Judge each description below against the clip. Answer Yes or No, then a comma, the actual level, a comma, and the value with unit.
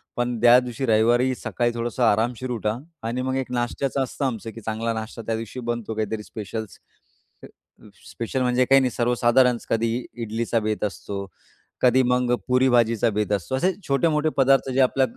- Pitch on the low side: Yes, low, 120 Hz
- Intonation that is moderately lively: No, narrow, 2.2 semitones